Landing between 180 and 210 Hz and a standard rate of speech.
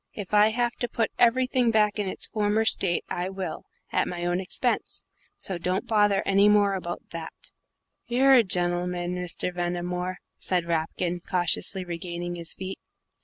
Yes: medium, 185 Hz; average, 160 wpm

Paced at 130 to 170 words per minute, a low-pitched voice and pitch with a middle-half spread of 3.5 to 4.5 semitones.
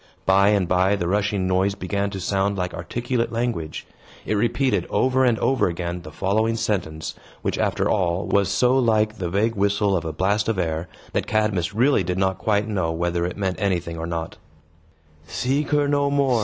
No: average, 190 wpm; low, 100 Hz; average, 3.9 semitones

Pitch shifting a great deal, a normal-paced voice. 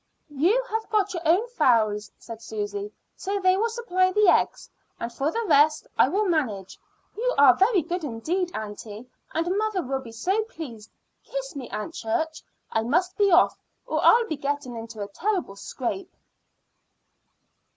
Yes: wide, 9.0 semitones; average, 165 wpm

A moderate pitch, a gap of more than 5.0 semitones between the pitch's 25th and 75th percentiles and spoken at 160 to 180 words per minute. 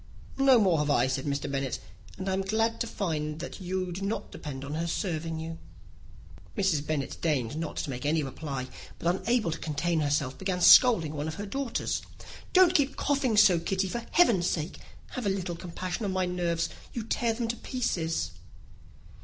No: medium, 175 Hz; wide, 5.4 semitones; average, 190 wpm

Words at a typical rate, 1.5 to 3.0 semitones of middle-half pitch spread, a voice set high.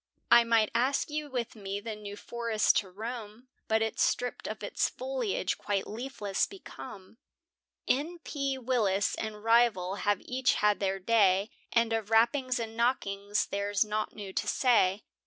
No: average, 155 wpm; average, 3.4 semitones; high, 225 Hz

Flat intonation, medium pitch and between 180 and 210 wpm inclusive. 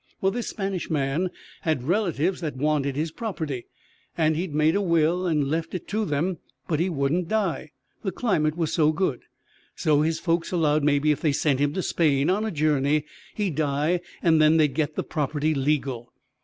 No: average, 3.1 semitones; medium, 155 Hz; average, 190 wpm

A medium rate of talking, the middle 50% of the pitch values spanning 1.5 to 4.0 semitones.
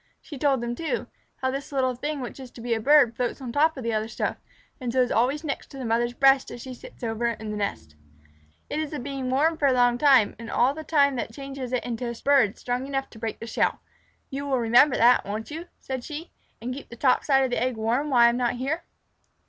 No: fast, 260 wpm; average, 2.9 semitones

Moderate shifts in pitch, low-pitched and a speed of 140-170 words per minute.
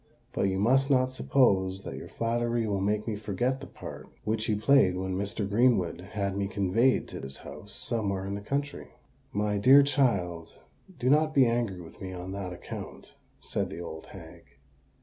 No: average, 4.4 semitones; low, 105 Hz; average, 185 wpm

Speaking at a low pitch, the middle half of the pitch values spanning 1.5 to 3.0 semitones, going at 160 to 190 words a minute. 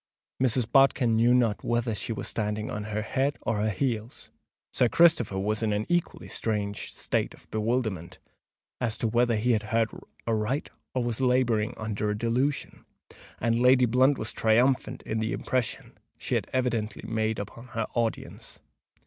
Yes: low, 115 Hz; average, 2.7 semitones; average, 165 wpm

